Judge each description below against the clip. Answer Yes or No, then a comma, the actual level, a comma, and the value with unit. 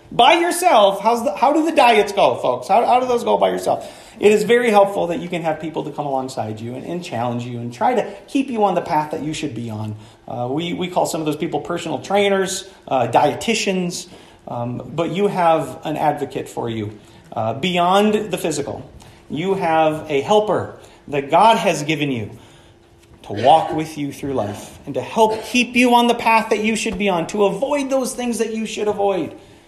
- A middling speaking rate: No, fast, 215 wpm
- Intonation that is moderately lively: No, wide, 7.5 semitones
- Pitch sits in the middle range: Yes, medium, 175 Hz